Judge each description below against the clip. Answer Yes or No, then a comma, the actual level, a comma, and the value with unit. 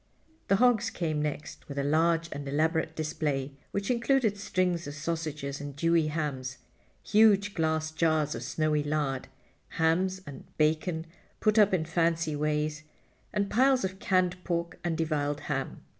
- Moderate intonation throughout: Yes, average, 3.5 semitones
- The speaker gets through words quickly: No, average, 150 wpm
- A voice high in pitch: No, medium, 160 Hz